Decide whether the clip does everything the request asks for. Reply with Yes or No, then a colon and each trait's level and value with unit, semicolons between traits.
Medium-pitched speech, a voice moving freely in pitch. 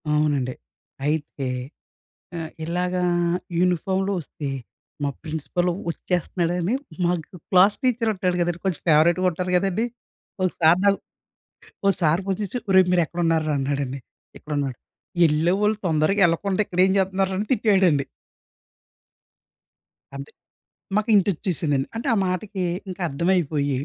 No: medium, 175 Hz; average, 3.7 semitones